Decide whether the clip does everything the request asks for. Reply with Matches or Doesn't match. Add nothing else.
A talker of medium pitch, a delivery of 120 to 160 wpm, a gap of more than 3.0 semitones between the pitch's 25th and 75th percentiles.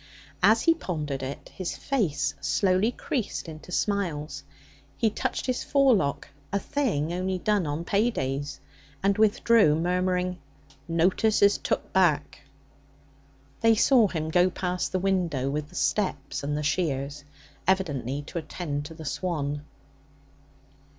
Matches